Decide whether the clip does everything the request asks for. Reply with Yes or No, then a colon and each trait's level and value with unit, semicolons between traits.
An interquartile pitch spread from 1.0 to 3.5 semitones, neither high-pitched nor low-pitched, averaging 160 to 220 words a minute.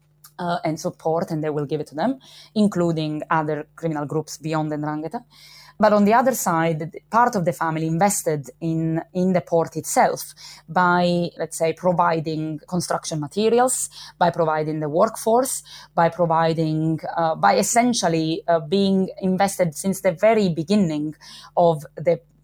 No: average, 2.8 semitones; medium, 165 Hz; average, 150 wpm